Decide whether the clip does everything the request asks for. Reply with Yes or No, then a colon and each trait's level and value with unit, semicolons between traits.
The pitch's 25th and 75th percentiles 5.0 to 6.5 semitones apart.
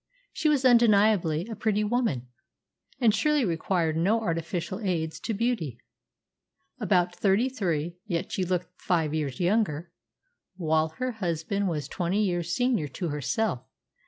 Yes: average, 5.3 semitones